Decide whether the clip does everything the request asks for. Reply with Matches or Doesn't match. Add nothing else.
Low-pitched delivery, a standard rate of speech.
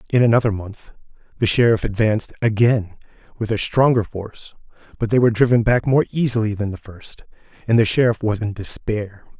Matches